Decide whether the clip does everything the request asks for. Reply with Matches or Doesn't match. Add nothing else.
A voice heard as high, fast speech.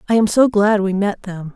Matches